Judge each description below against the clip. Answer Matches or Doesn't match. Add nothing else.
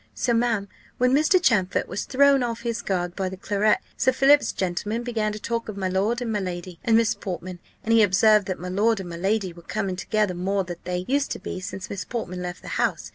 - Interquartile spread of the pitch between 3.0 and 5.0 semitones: Matches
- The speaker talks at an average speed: Doesn't match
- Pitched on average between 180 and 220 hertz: Matches